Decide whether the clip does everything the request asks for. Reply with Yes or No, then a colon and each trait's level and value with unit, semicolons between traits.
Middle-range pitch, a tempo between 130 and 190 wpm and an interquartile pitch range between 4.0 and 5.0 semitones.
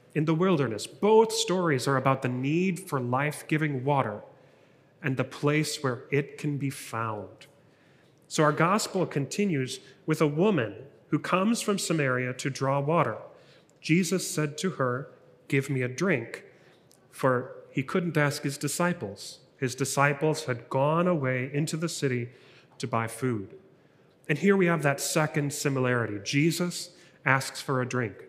Yes: medium, 145 Hz; average, 155 wpm; average, 4.3 semitones